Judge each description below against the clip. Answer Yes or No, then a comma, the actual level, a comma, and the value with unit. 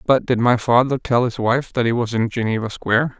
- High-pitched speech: No, low, 120 Hz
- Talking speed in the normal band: No, fast, 245 wpm